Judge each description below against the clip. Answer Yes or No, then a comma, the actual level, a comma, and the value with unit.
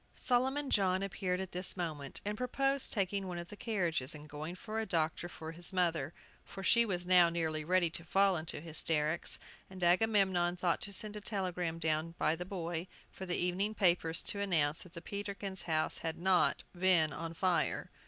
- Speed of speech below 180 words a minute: No, average, 190 wpm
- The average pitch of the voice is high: No, medium, 180 Hz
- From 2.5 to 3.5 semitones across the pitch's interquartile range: Yes, average, 3.0 semitones